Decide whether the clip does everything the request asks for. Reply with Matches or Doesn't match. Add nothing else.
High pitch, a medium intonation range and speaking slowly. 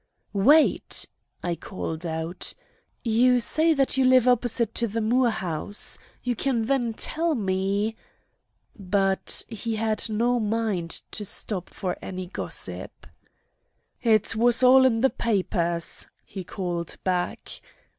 Matches